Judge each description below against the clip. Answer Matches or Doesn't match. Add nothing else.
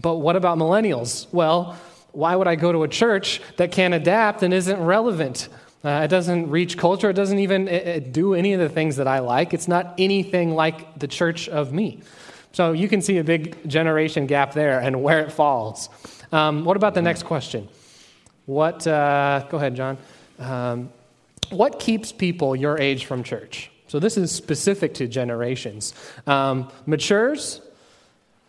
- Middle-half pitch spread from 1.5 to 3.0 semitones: Doesn't match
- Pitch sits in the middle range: Matches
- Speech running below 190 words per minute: Matches